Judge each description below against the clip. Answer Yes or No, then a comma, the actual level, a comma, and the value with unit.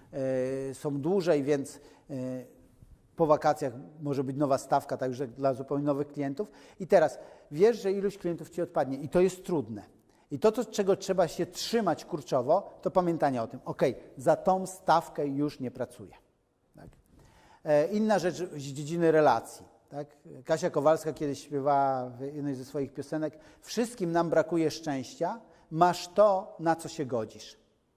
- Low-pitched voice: No, medium, 150 Hz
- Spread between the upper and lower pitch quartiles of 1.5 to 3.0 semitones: No, average, 3.9 semitones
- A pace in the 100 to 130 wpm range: No, average, 150 wpm